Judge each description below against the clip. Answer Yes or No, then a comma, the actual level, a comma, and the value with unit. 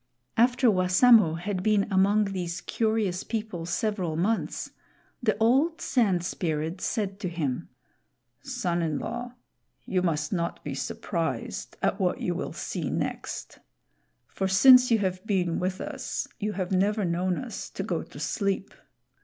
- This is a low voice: No, high, 190 Hz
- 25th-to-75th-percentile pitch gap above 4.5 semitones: No, average, 4.2 semitones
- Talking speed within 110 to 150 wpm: Yes, average, 145 wpm